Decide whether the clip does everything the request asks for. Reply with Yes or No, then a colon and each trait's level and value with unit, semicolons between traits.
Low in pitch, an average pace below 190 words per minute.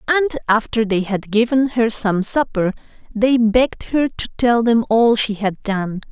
No: high, 225 Hz; average, 175 wpm